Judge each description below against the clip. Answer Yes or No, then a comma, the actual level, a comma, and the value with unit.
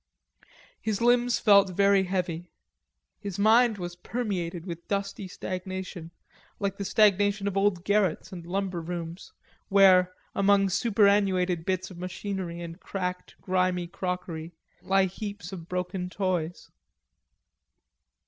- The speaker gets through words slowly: Yes, slow, 120 wpm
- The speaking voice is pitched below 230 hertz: Yes, medium, 185 Hz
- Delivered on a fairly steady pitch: Yes, narrow, 2.2 semitones